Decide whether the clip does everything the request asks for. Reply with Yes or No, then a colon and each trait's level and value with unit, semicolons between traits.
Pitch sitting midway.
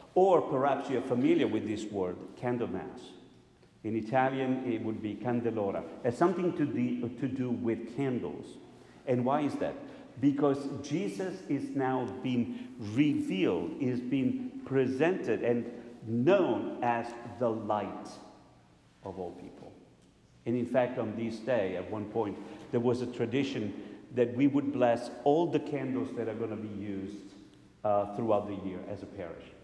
No: low, 120 Hz